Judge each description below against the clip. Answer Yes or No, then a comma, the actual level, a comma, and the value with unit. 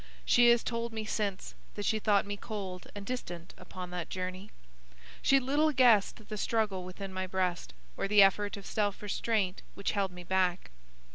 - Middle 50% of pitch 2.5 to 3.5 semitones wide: Yes, average, 2.9 semitones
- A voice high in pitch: Yes, high, 200 Hz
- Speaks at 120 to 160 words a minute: No, average, 180 wpm